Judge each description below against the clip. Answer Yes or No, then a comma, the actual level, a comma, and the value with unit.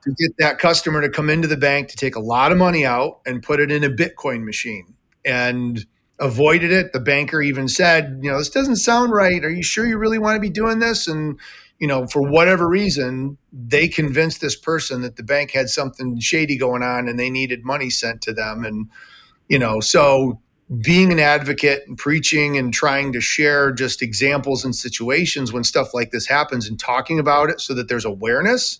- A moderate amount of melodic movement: Yes, average, 4.3 semitones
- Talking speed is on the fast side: Yes, fast, 210 wpm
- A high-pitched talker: No, medium, 140 Hz